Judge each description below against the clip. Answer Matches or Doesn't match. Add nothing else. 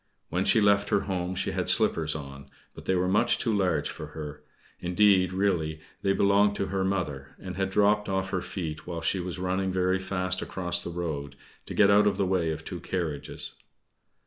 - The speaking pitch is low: Matches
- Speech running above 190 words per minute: Matches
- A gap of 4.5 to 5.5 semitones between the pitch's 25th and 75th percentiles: Doesn't match